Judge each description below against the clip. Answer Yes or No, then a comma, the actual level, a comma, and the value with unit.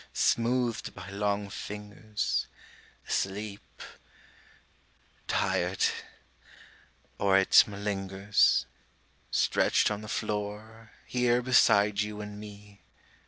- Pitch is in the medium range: No, low, 105 Hz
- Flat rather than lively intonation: Yes, narrow, 1.3 semitones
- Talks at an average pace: No, slow, 80 wpm